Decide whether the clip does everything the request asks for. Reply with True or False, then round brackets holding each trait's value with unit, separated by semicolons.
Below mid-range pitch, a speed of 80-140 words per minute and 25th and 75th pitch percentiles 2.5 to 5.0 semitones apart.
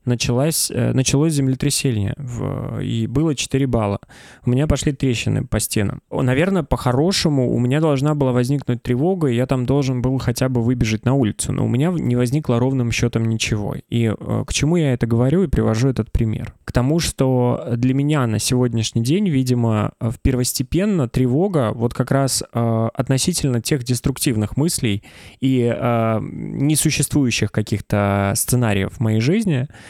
False (130 Hz; 150 wpm; 3.4 semitones)